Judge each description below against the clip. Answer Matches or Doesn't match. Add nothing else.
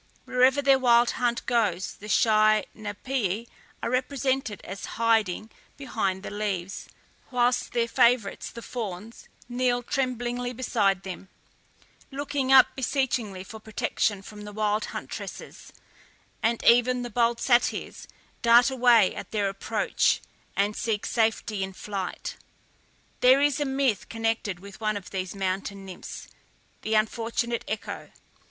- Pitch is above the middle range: Matches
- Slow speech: Matches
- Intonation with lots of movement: Doesn't match